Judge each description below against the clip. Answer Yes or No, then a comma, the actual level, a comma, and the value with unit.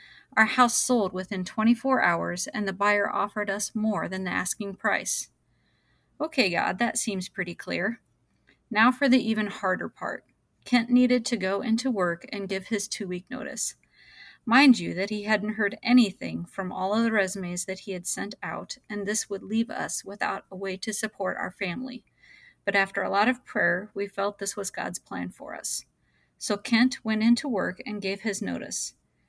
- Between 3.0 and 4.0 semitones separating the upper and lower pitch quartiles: Yes, average, 3.6 semitones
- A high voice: Yes, high, 210 Hz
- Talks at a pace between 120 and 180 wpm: No, average, 190 wpm